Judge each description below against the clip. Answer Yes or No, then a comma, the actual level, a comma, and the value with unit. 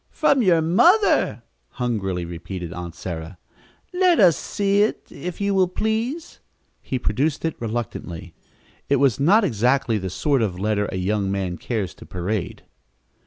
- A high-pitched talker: No, low, 120 Hz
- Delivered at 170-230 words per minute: No, average, 150 wpm